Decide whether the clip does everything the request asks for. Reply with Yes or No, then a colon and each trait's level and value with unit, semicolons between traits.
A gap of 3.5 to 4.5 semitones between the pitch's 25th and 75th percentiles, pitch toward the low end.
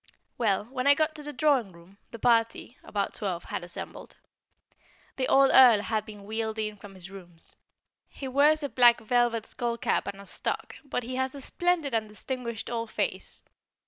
No: average, 4.1 semitones; high, 230 Hz